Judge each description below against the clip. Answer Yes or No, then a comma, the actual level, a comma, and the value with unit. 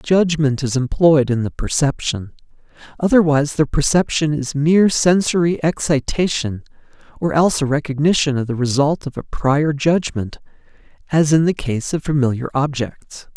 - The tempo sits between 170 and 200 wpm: No, average, 140 wpm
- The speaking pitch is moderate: Yes, medium, 145 Hz